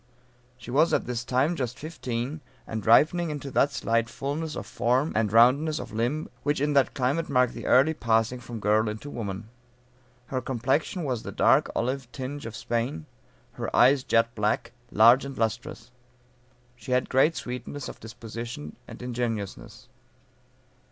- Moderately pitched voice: No, low, 125 Hz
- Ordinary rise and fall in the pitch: Yes, average, 3.5 semitones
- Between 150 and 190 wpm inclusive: Yes, average, 160 wpm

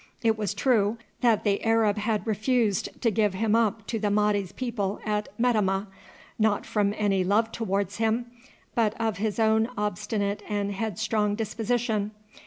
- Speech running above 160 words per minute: No, average, 155 wpm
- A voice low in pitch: No, high, 215 Hz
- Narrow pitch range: Yes, narrow, 1.7 semitones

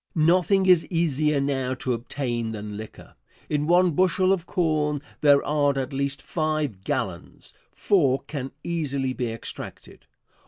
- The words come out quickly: No, average, 140 wpm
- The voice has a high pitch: No, medium, 145 Hz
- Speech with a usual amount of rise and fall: Yes, average, 4.0 semitones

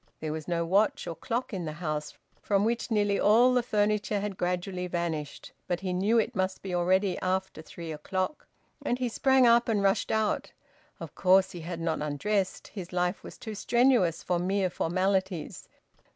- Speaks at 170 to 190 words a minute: Yes, average, 180 wpm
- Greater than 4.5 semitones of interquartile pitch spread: No, average, 3.3 semitones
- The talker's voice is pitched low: No, high, 190 Hz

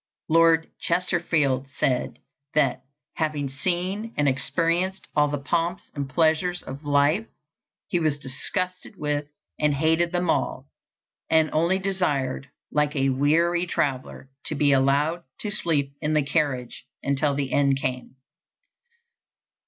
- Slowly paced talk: Yes, slow, 130 wpm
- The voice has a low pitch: No, medium, 150 Hz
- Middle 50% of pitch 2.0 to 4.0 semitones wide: Yes, average, 3.7 semitones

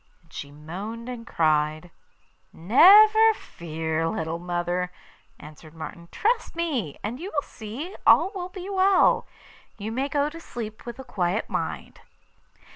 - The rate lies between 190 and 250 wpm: No, average, 140 wpm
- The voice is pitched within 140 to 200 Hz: No, high, 215 Hz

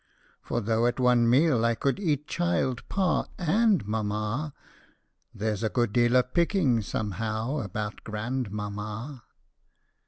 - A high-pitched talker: No, low, 120 Hz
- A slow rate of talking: Yes, slow, 130 wpm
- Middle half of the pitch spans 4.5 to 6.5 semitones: Yes, average, 5.1 semitones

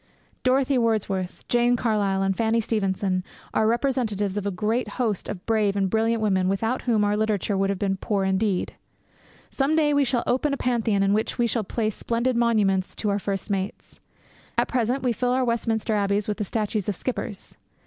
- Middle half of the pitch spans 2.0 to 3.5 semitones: Yes, average, 3.2 semitones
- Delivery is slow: No, average, 190 wpm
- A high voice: Yes, high, 215 Hz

